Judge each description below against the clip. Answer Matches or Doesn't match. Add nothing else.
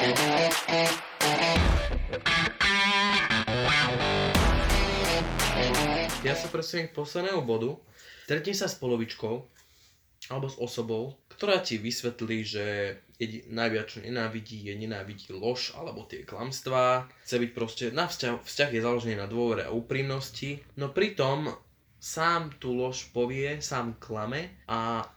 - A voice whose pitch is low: Matches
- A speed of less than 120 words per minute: Matches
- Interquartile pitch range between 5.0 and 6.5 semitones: Doesn't match